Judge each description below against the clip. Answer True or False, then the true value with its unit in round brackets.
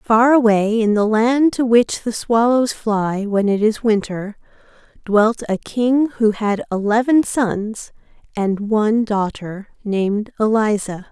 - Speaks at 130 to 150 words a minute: True (140 wpm)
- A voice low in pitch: False (220 Hz)